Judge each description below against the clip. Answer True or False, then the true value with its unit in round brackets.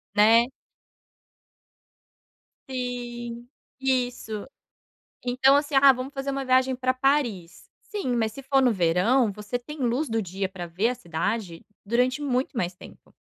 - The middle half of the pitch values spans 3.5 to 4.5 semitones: True (3.9 semitones)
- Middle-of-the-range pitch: False (245 Hz)